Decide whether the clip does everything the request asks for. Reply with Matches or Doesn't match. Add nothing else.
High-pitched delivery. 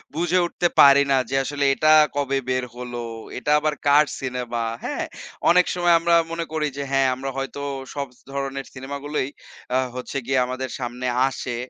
Doesn't match